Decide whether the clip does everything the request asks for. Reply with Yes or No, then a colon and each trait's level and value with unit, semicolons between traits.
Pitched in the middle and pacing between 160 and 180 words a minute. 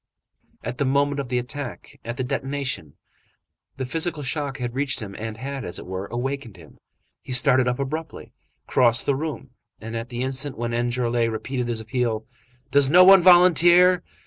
No: low, 130 Hz; average, 175 wpm